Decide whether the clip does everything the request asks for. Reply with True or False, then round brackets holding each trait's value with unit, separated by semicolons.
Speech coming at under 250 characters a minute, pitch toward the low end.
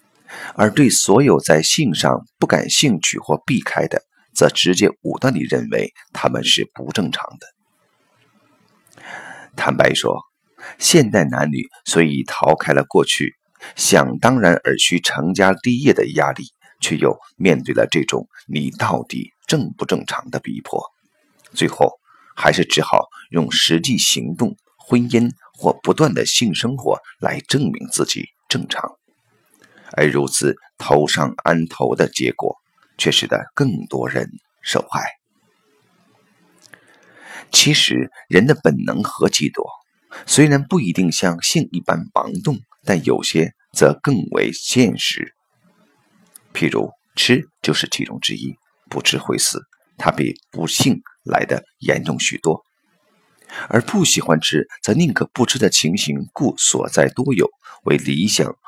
True (195 characters per minute; 90 Hz)